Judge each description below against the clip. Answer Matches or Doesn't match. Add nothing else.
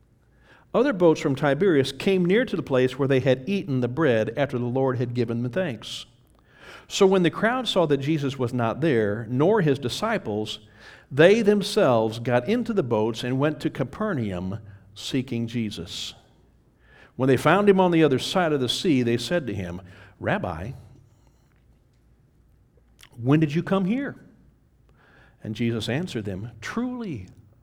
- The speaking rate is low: Doesn't match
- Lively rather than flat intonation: Matches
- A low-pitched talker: Matches